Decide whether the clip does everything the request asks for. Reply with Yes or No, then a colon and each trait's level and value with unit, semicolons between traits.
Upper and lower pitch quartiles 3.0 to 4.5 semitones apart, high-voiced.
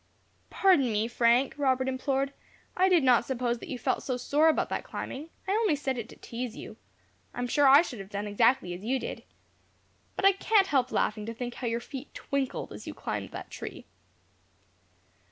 Yes: average, 3.3 semitones; very high, 260 Hz